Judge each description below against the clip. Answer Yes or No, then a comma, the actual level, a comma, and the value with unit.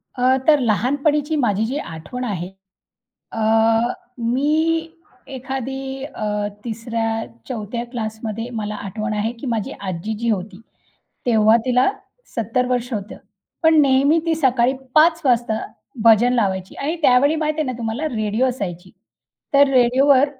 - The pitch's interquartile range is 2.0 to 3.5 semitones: No, average, 3.9 semitones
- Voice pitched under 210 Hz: No, high, 240 Hz